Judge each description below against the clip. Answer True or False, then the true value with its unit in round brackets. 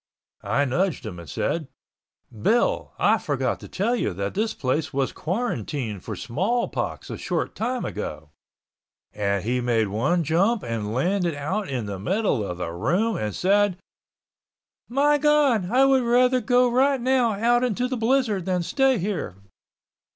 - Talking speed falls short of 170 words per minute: True (155 wpm)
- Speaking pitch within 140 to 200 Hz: True (190 Hz)